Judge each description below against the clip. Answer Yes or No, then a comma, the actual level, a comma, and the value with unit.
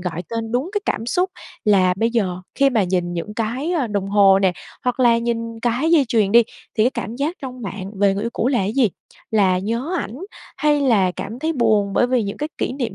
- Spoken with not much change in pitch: No, average, 4.3 semitones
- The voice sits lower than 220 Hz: No, high, 230 Hz